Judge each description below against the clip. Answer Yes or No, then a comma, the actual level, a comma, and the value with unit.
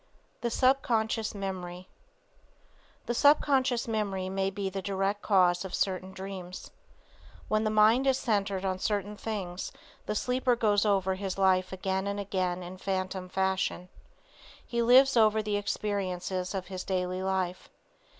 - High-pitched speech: Yes, high, 195 Hz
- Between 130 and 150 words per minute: Yes, average, 140 wpm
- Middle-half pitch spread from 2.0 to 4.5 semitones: Yes, narrow, 2.5 semitones